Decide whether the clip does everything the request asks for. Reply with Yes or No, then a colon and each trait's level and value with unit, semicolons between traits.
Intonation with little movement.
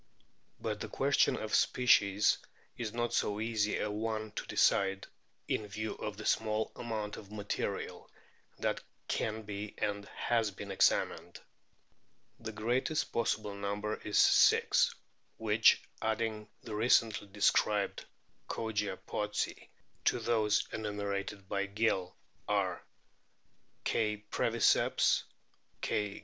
Yes: narrow, 1.5 semitones